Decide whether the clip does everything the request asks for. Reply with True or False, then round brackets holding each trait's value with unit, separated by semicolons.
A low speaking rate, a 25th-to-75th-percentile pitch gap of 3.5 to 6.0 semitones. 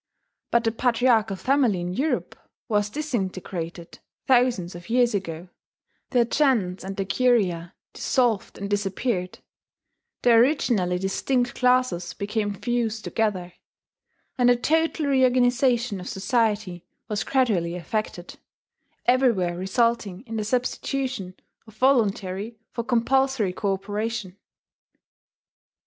True (105 wpm; 4.5 semitones)